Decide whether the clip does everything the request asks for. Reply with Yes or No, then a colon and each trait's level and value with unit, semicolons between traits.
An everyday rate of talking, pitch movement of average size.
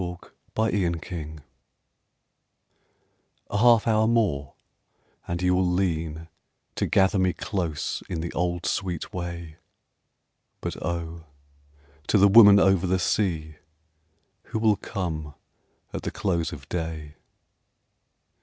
No: slow, 120 wpm; average, 3.0 semitones